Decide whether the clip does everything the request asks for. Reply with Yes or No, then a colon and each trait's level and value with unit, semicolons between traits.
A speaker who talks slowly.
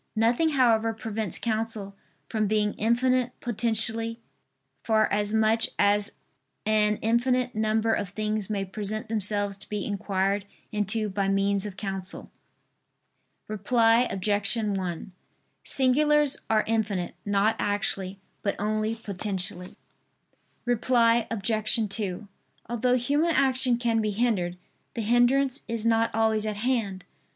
Yes: slow, 120 wpm